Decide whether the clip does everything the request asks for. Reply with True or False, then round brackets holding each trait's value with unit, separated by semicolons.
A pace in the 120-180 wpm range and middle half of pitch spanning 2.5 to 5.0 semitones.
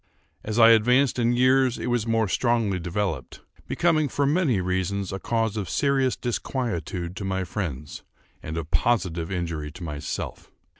False (155 wpm; 5.6 semitones)